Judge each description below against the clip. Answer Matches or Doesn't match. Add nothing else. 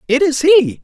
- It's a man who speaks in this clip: Matches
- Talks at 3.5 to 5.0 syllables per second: Matches